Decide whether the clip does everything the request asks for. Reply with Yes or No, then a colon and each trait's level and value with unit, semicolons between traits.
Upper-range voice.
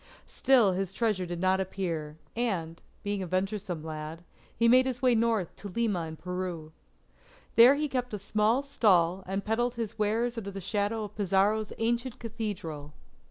Yes: high, 205 Hz